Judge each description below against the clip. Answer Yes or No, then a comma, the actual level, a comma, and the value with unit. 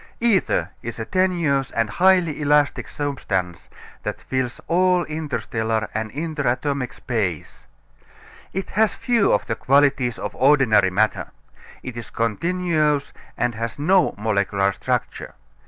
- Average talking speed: No, slow, 125 wpm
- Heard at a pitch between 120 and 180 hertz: Yes, medium, 140 Hz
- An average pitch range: No, wide, 6.8 semitones